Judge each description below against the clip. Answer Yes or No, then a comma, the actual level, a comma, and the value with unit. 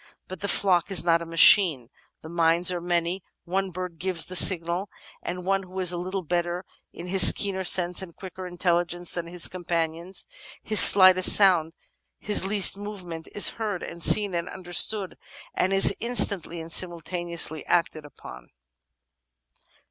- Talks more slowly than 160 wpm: No, average, 165 wpm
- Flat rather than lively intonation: Yes, narrow, 1.9 semitones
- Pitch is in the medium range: Yes, medium, 180 Hz